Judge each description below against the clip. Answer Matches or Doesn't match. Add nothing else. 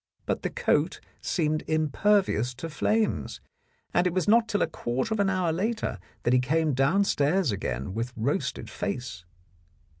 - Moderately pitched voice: Matches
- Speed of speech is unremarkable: Matches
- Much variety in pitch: Matches